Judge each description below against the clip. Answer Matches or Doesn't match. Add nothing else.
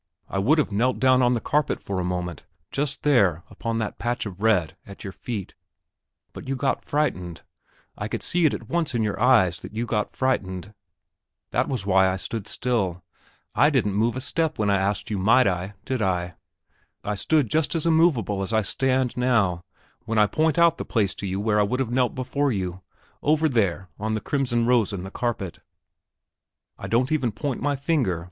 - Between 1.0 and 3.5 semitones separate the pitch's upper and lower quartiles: Doesn't match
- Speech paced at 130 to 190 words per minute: Doesn't match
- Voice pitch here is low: Matches